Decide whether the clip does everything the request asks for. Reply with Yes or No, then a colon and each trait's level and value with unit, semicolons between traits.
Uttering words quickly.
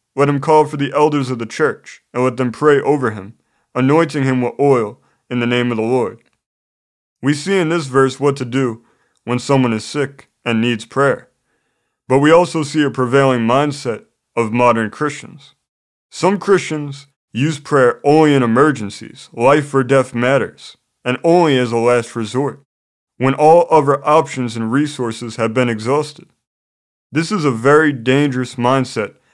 No: average, 170 wpm